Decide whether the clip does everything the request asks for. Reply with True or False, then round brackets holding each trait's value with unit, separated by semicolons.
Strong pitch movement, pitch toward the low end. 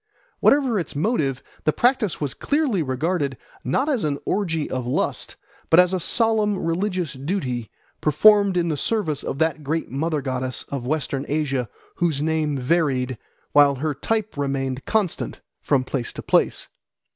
False (5.8 semitones; 155 Hz)